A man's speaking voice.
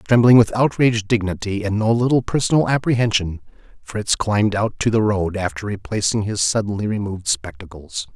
Yes: male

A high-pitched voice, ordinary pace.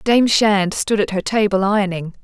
Yes: high, 200 Hz; average, 190 wpm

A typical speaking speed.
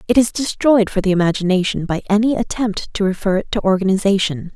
Yes: average, 185 wpm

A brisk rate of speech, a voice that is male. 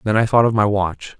Yes: fast, 300 wpm; male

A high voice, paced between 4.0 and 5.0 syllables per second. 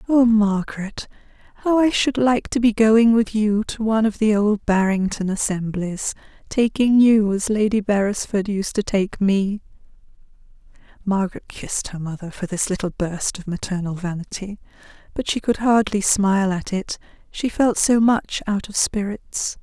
Yes: high, 205 Hz; 4.6 syllables/s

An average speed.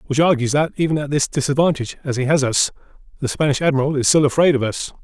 No: fast, 225 wpm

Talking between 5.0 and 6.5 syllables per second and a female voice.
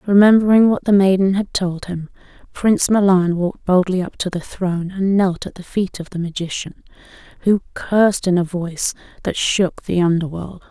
Yes: 5.2 syllables/s; female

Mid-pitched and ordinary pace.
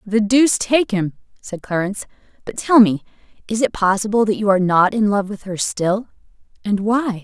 No: high, 210 Hz; average, 180 wpm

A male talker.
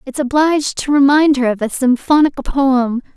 No: female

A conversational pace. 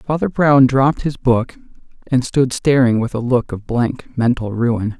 Yes: average, 180 wpm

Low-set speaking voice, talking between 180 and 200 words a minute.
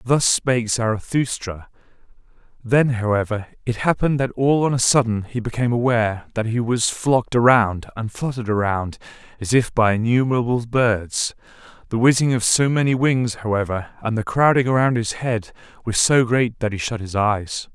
No: low, 115 Hz; average, 160 wpm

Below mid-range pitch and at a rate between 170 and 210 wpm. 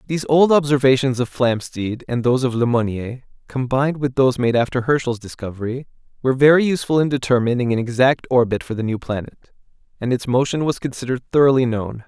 Yes: low, 125 Hz; average, 180 wpm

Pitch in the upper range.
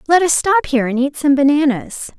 Yes: very high, 285 Hz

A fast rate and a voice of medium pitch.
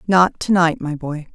No: average, 180 wpm; medium, 165 Hz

